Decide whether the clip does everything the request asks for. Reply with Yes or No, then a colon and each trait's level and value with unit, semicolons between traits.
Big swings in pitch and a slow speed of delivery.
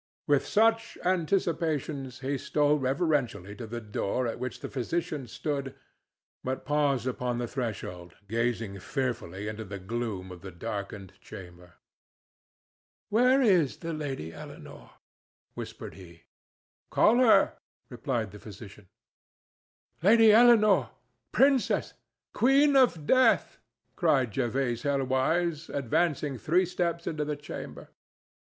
Yes: wide, 7.2 semitones; slow, 115 wpm